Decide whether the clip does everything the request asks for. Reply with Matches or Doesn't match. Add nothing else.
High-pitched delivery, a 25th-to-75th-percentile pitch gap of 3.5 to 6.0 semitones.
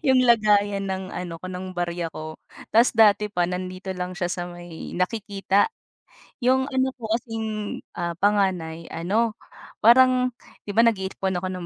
Matches